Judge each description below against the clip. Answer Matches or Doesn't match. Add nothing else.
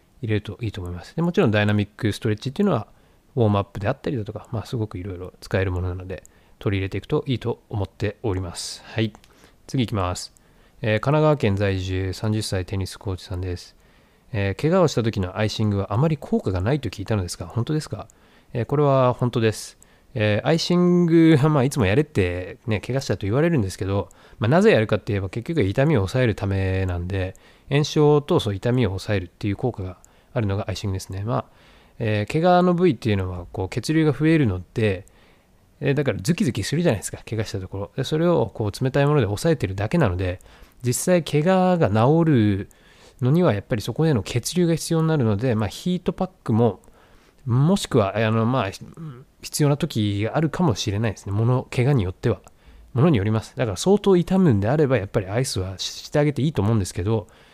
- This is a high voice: Doesn't match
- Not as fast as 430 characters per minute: Doesn't match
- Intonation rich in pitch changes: Matches